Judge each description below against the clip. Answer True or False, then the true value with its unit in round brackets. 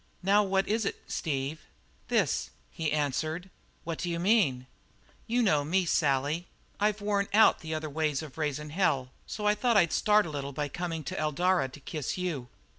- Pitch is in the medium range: True (160 Hz)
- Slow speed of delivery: False (180 wpm)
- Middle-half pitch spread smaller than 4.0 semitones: False (4.8 semitones)